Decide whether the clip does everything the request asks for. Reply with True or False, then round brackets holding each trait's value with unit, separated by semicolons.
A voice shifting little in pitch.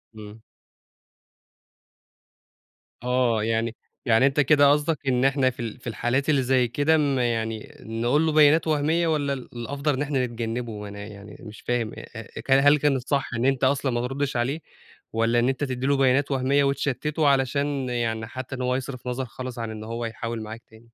False (3.3 semitones)